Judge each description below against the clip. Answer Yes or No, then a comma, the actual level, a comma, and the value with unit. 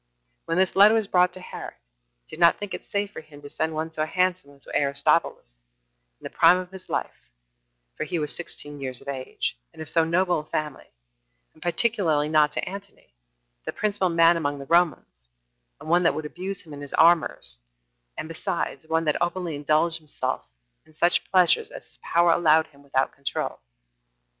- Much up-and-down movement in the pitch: No, average, 3.3 semitones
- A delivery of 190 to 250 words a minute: Yes, average, 195 wpm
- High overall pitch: No, medium, 160 Hz